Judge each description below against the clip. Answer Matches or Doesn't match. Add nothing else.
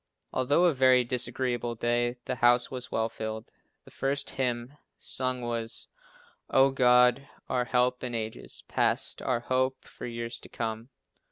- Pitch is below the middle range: Matches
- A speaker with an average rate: Matches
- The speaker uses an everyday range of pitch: Doesn't match